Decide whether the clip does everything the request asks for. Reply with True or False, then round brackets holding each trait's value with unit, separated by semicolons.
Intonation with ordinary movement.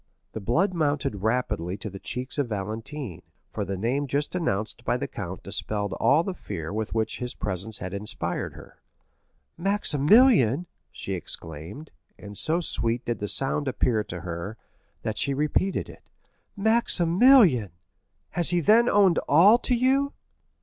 False (9.0 semitones)